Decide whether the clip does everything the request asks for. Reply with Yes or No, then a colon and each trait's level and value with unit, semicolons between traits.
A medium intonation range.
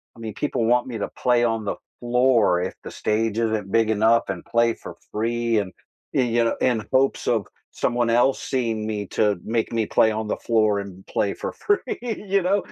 No: narrow, 2.2 semitones